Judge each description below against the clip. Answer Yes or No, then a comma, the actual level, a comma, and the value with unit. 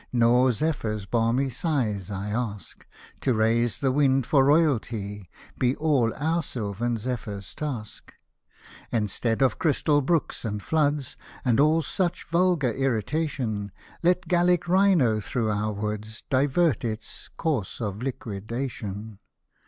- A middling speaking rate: No, slow, 130 wpm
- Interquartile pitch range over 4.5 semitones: Yes, wide, 5.5 semitones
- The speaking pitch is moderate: No, low, 125 Hz